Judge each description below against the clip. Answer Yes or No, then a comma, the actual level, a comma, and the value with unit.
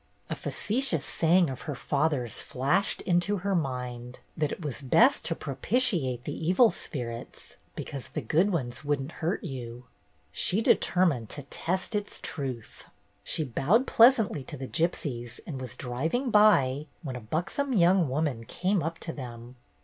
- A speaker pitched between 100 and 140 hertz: No, medium, 150 Hz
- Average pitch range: No, wide, 6.4 semitones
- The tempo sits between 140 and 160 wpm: Yes, average, 155 wpm